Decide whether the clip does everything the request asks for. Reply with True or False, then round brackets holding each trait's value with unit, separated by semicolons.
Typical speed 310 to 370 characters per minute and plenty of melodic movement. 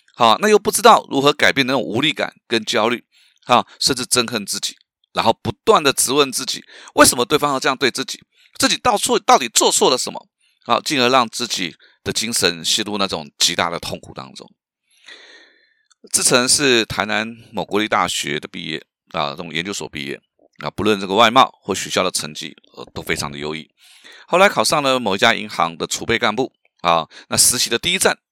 False (300 characters per minute; 6.3 semitones)